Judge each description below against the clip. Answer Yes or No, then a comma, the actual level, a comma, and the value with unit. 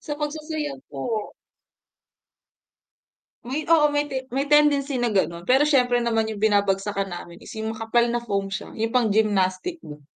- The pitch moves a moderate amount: No, wide, 6.0 semitones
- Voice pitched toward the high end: Yes, high, 225 Hz